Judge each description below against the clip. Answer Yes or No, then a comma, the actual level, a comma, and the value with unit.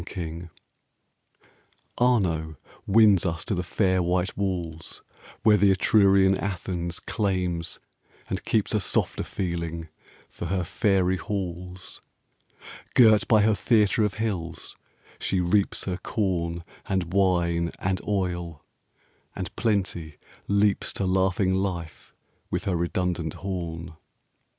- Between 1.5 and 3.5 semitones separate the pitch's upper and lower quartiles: Yes, narrow, 2.5 semitones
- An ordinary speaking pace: No, slow, 115 wpm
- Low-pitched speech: Yes, very low, 95 Hz